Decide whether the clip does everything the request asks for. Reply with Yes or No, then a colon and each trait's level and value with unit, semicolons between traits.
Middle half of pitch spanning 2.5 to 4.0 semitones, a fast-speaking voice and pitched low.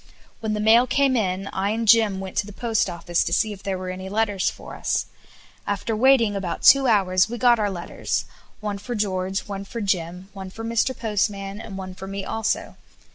No: average, 2.8 semitones; fast, 210 wpm; high, 205 Hz